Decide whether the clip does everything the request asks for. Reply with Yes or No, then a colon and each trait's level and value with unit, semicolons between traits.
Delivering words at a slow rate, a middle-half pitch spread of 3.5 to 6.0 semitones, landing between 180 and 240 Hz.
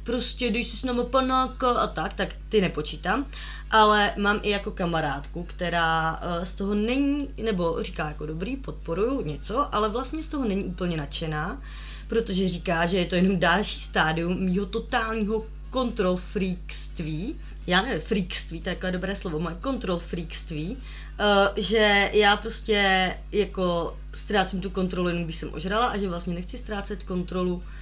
No: average, 155 wpm; average, 4.1 semitones; high, 190 Hz